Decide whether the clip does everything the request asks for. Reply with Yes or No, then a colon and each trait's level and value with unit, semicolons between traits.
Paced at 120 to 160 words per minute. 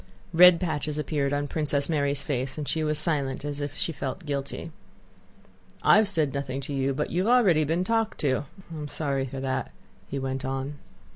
No: fast, 205 wpm